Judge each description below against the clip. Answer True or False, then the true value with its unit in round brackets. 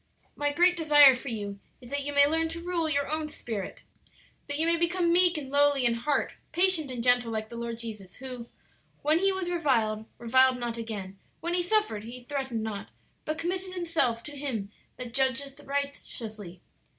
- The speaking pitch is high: True (275 Hz)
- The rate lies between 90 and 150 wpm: False (185 wpm)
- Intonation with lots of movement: True (5.7 semitones)